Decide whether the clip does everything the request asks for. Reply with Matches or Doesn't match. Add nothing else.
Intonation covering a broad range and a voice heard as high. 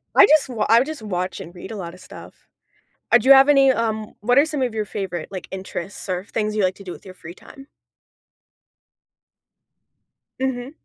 Matches